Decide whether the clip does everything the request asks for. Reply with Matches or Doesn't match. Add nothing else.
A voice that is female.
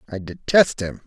Doesn't match